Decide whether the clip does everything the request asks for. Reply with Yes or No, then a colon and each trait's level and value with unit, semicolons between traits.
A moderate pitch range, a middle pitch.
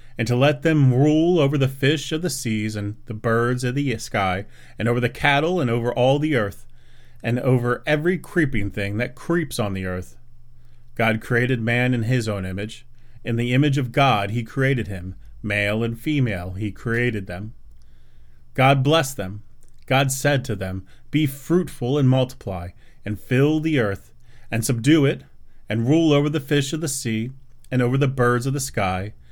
No: average, 4.5 semitones; low, 120 Hz